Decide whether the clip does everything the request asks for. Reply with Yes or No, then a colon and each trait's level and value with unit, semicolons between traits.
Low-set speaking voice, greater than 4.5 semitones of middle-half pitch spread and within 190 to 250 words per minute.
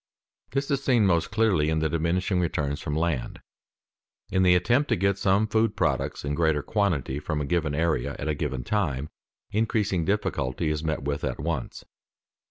No: very low, 85 Hz; average, 5.1 semitones; average, 180 wpm